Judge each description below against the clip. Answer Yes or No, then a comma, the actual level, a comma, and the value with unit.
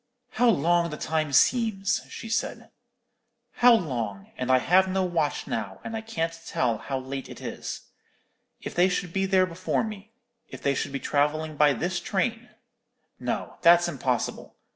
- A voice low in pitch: No, medium, 170 Hz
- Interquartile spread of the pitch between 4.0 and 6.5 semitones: Yes, wide, 5.6 semitones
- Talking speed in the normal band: Yes, average, 165 wpm